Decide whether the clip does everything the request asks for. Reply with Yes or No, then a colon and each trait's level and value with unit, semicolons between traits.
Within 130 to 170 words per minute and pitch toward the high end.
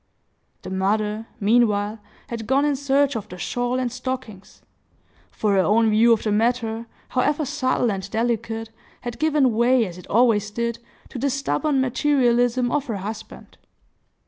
Yes: average, 155 wpm; high, 235 Hz